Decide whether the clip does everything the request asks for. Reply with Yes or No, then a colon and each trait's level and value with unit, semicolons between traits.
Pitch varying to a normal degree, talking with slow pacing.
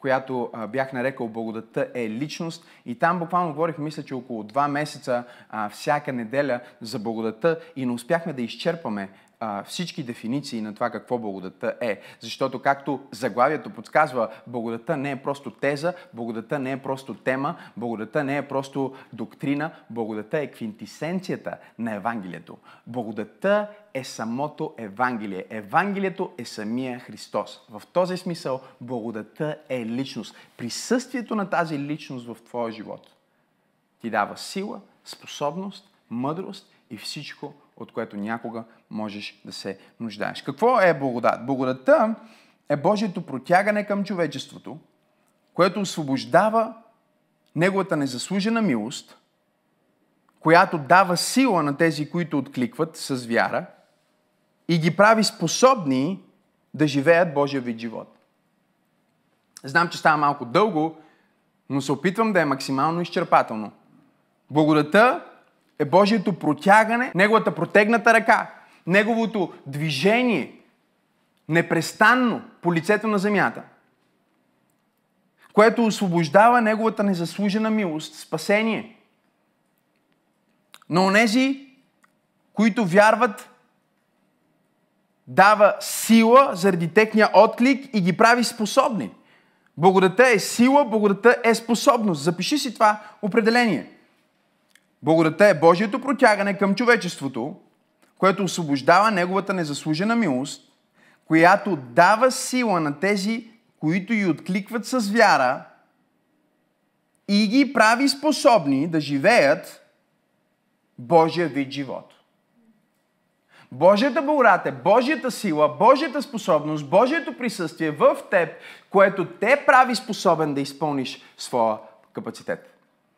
No: wide, 7.9 semitones; slow, 110 wpm